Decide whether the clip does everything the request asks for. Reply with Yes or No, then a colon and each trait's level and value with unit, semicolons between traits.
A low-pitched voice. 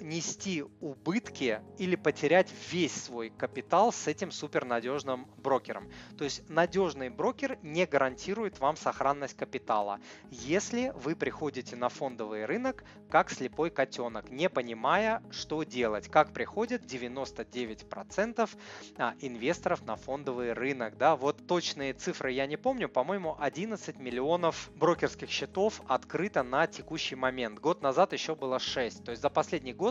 No: medium, 150 Hz